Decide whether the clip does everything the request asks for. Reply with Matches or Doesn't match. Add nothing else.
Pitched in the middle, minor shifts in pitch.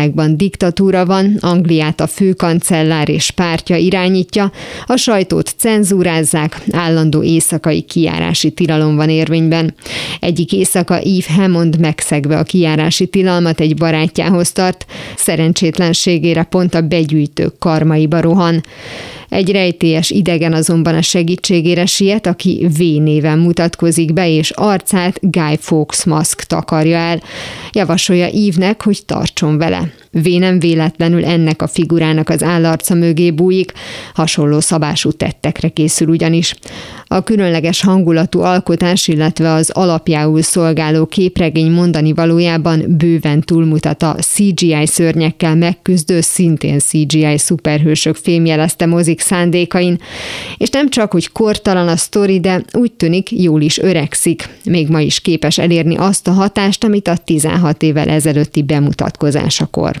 Matches